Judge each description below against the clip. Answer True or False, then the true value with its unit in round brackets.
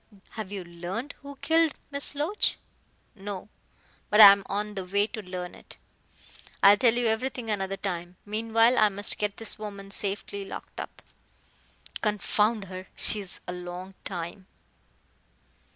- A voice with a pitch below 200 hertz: False (205 Hz)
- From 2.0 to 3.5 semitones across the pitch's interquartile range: True (2.6 semitones)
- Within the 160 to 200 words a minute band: False (150 wpm)